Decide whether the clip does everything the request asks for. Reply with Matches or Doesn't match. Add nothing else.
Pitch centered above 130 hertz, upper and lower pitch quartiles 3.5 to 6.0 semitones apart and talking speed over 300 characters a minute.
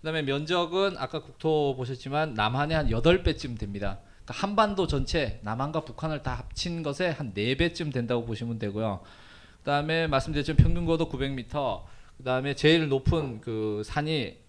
Matches